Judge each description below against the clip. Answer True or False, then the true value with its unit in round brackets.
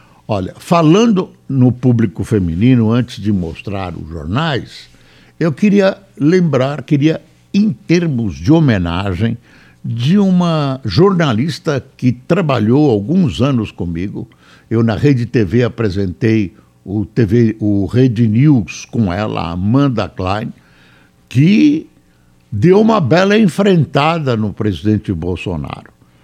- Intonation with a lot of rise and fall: True (7.5 semitones)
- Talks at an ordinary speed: False (110 wpm)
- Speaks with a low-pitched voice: True (120 Hz)